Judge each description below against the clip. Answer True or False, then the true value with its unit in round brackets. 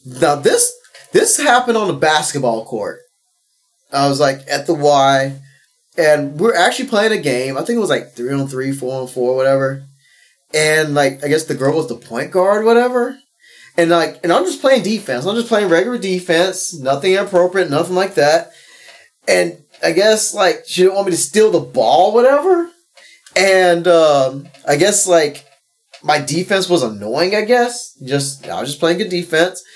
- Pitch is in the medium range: True (175 Hz)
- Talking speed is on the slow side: False (185 wpm)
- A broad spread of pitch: True (7.5 semitones)